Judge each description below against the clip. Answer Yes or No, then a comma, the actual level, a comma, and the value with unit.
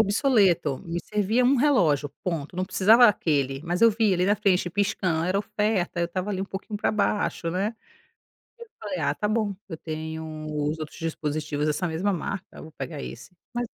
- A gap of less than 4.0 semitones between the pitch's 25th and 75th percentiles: No, average, 4.6 semitones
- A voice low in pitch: No, medium, 185 Hz